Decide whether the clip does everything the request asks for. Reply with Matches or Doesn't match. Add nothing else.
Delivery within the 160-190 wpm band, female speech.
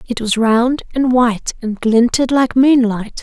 Matches